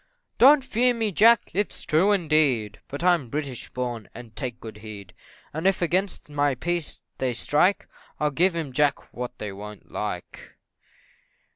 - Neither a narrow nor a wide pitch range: No, wide, 6.9 semitones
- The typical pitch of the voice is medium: Yes, medium, 150 Hz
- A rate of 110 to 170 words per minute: Yes, average, 155 wpm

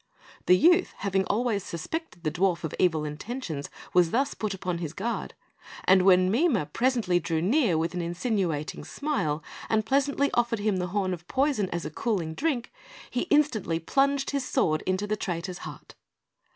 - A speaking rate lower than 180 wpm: Yes, average, 165 wpm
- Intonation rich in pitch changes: Yes, wide, 6.5 semitones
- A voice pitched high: Yes, high, 195 Hz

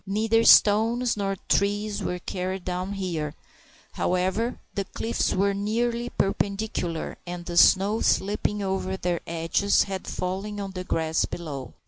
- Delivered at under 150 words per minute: Yes, average, 140 wpm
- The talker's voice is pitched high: Yes, high, 195 Hz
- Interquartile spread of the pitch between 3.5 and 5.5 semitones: No, narrow, 2.5 semitones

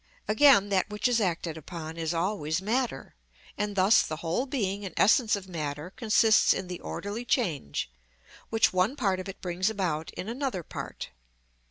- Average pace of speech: Yes, average, 170 wpm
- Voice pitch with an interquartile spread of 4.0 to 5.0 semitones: Yes, average, 4.5 semitones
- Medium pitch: No, high, 195 Hz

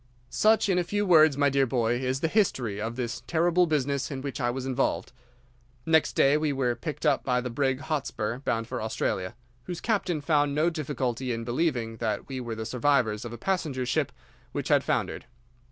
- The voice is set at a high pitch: No, low, 135 Hz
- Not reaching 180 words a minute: No, average, 200 wpm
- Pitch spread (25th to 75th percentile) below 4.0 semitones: No, average, 4.5 semitones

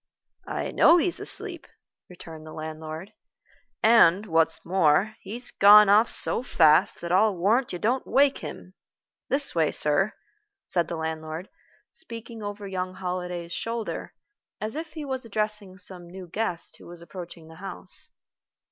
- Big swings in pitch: No, average, 4.6 semitones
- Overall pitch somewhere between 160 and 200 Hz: Yes, medium, 185 Hz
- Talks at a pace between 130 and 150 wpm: Yes, average, 145 wpm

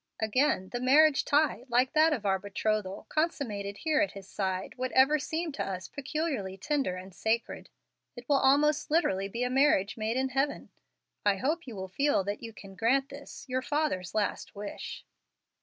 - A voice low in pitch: No, very high, 250 Hz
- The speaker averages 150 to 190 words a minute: Yes, average, 180 wpm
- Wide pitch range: Yes, wide, 6.4 semitones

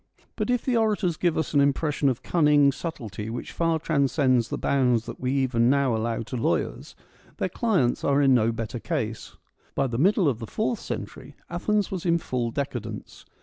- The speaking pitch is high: No, medium, 140 Hz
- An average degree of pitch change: No, wide, 6.0 semitones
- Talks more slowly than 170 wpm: No, average, 190 wpm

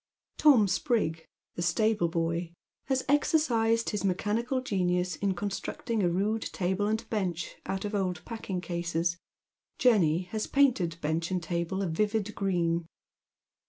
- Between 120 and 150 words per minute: Yes, average, 140 wpm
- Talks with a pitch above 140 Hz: Yes, high, 190 Hz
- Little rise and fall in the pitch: No, average, 4.3 semitones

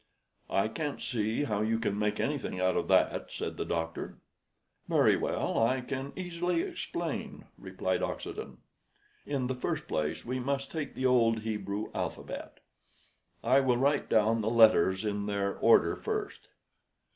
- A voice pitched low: Yes, low, 115 Hz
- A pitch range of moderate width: Yes, average, 4.5 semitones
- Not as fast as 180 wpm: Yes, average, 150 wpm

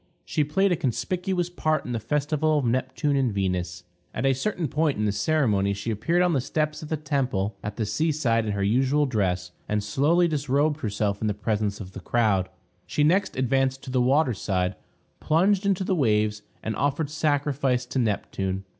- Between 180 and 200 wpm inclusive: Yes, average, 195 wpm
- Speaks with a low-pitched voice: Yes, low, 130 Hz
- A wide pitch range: Yes, wide, 6.5 semitones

